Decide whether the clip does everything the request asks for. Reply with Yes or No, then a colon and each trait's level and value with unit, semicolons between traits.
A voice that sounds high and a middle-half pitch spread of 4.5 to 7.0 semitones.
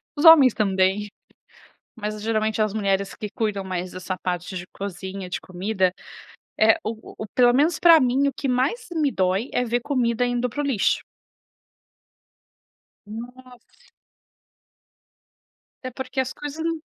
Yes: high, 225 Hz; average, 4.8 semitones